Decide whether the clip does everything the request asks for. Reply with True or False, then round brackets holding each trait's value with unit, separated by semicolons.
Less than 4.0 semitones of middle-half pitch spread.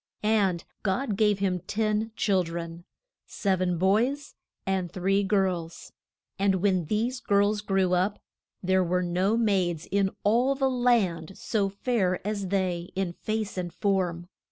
True (2.8 semitones)